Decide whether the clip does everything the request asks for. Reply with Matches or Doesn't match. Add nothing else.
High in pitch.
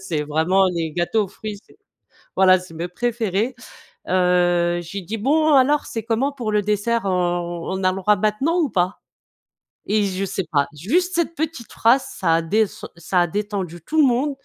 Matches